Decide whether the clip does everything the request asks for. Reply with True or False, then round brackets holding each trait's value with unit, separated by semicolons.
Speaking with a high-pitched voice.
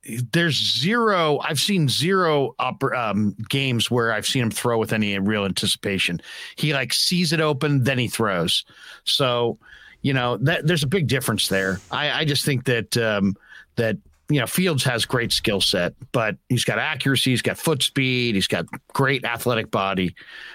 False (125 Hz)